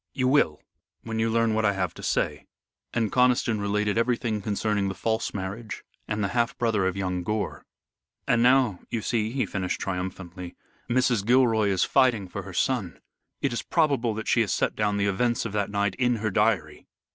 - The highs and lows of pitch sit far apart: No, average, 3.3 semitones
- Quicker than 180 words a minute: Yes, average, 190 wpm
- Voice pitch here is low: Yes, low, 110 Hz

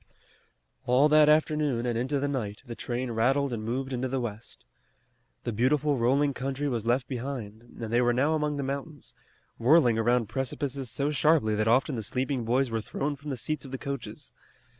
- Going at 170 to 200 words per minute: Yes, average, 190 wpm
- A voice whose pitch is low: Yes, low, 130 Hz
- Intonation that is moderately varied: Yes, average, 3.2 semitones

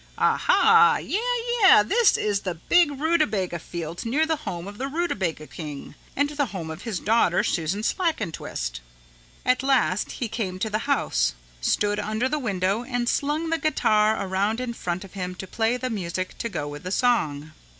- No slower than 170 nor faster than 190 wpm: Yes, average, 180 wpm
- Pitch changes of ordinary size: No, wide, 7.1 semitones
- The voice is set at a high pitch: Yes, high, 215 Hz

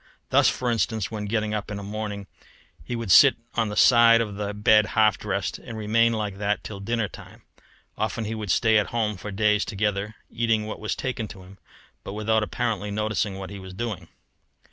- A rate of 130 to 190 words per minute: No, fast, 205 wpm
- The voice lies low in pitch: Yes, low, 105 Hz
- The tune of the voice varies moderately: No, narrow, 1.7 semitones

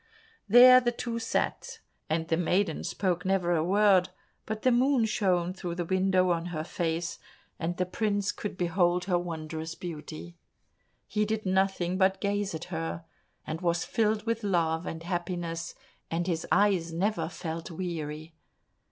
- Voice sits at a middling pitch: Yes, medium, 180 Hz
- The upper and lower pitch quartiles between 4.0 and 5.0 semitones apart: No, average, 3.4 semitones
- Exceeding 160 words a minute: No, average, 155 wpm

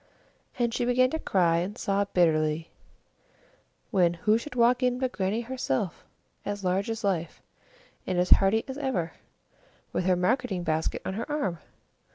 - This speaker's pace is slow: No, average, 160 wpm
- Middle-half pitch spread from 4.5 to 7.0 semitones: Yes, wide, 5.6 semitones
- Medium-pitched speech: No, high, 200 Hz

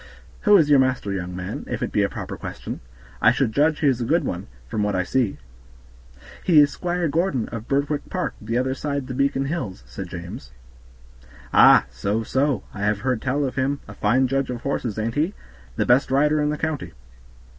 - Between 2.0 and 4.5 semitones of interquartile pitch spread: No, wide, 5.5 semitones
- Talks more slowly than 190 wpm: No, fast, 205 wpm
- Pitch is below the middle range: Yes, low, 130 Hz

